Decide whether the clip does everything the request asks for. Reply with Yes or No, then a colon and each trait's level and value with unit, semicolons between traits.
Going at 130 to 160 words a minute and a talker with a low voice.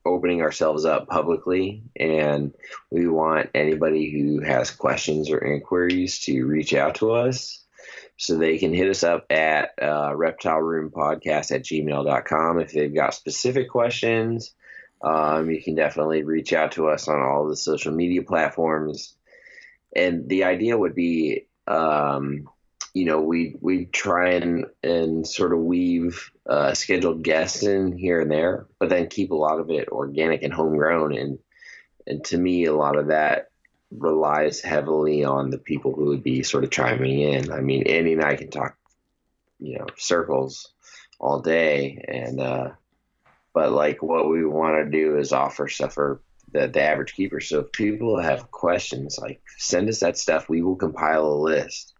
No: average, 170 wpm; very low, 80 Hz